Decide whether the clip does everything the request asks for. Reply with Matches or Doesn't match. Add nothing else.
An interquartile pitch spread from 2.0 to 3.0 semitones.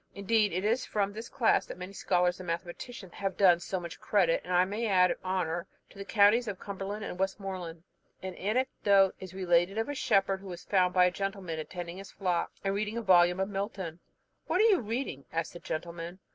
Matches